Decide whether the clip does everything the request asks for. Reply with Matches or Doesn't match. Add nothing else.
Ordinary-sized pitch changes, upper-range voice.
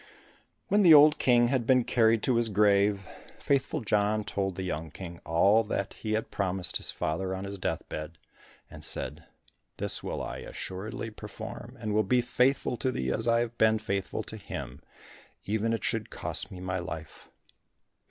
Doesn't match